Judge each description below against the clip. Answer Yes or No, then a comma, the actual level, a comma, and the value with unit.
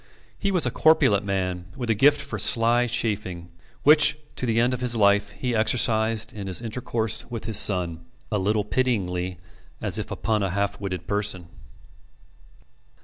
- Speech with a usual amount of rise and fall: Yes, average, 3.8 semitones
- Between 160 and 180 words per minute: Yes, average, 165 wpm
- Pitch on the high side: No, low, 110 Hz